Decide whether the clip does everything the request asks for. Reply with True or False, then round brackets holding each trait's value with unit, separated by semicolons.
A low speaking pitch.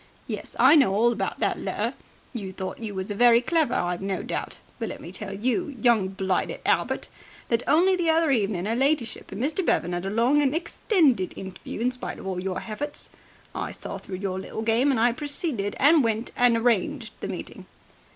False (230 Hz)